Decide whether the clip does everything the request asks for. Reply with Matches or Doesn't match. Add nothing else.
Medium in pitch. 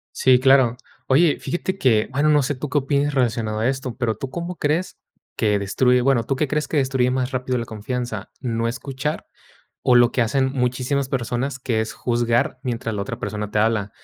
Doesn't match